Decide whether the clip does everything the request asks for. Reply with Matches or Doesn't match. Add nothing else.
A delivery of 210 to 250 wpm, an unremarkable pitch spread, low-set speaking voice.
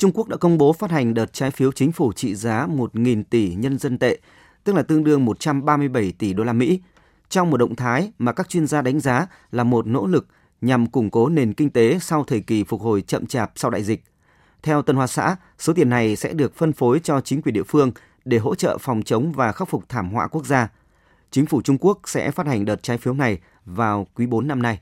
Matches